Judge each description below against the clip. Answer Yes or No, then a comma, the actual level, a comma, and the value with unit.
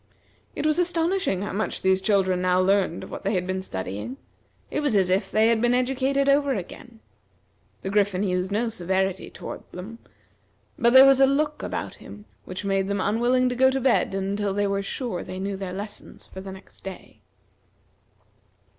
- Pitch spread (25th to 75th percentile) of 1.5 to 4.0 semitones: No, average, 5.0 semitones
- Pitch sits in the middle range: No, high, 205 Hz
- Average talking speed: Yes, average, 190 wpm